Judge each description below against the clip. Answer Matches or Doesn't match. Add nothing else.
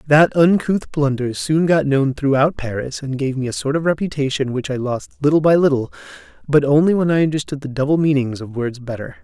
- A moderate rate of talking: Doesn't match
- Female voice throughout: Doesn't match